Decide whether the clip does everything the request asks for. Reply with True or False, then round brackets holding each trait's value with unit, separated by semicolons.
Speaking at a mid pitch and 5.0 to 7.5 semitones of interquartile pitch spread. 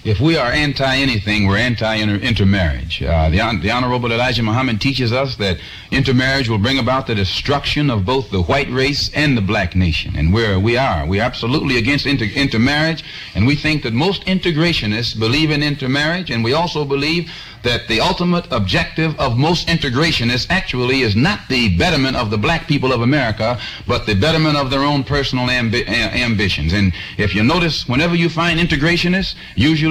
False (130 Hz; 5.5 semitones)